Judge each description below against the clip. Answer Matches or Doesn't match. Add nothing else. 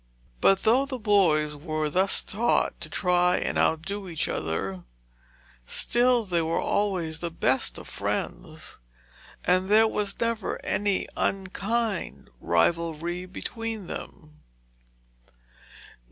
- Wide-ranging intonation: Doesn't match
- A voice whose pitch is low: Doesn't match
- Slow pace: Matches